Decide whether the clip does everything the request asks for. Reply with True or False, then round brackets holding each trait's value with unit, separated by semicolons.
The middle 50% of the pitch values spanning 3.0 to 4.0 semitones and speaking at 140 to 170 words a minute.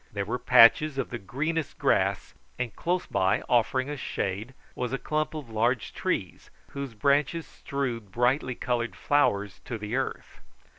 True (3.7 semitones; 155 wpm)